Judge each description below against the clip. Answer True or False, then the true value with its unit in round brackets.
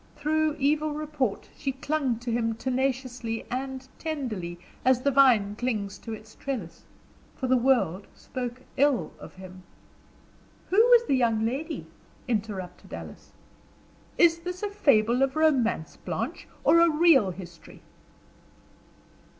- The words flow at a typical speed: False (130 wpm)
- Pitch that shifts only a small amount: False (5.1 semitones)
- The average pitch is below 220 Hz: False (255 Hz)